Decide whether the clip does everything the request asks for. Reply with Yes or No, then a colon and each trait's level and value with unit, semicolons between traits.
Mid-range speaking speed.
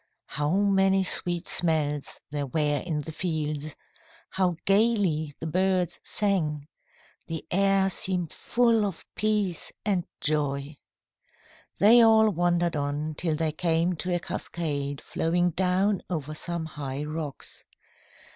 No: slow, 125 wpm